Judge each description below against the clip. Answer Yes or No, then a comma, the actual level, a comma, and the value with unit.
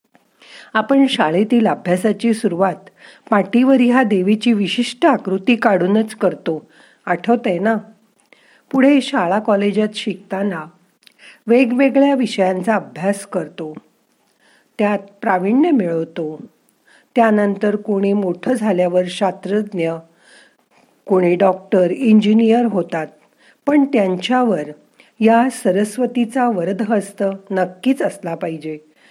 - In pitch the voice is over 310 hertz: No, high, 205 Hz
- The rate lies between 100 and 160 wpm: No, average, 85 wpm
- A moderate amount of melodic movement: Yes, average, 4.4 semitones